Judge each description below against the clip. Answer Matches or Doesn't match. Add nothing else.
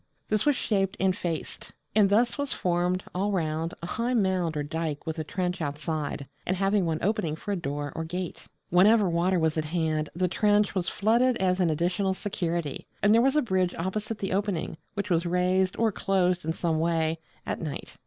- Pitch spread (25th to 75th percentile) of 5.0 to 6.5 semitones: Doesn't match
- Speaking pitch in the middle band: Matches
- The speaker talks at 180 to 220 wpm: Matches